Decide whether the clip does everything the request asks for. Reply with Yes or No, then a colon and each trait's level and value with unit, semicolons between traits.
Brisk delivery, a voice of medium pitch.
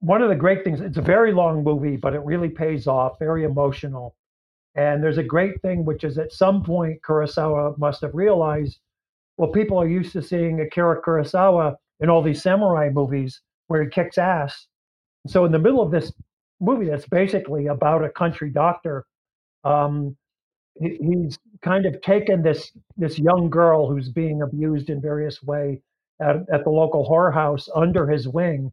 No: average, 180 wpm; medium, 160 Hz